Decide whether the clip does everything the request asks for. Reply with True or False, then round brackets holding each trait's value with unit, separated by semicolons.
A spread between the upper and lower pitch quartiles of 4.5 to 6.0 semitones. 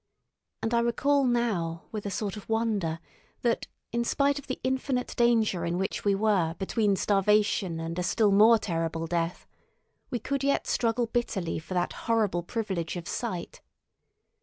True (5.1 semitones)